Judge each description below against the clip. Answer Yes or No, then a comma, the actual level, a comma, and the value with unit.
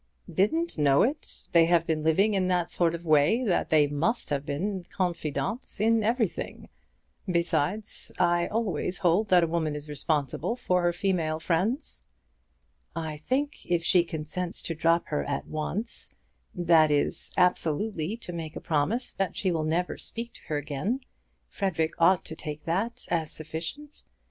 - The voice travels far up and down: No, average, 4.1 semitones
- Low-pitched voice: No, medium, 170 Hz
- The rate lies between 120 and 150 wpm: No, average, 160 wpm